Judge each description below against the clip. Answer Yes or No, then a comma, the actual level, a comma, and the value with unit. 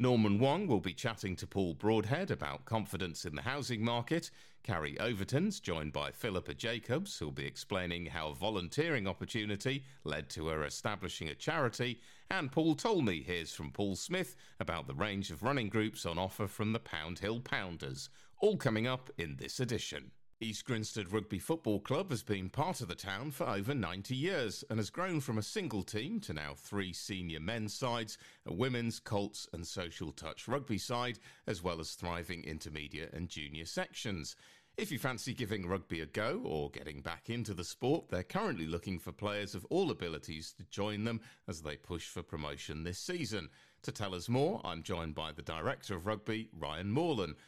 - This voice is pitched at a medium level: No, low, 105 Hz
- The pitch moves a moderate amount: No, wide, 6.0 semitones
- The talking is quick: No, average, 185 wpm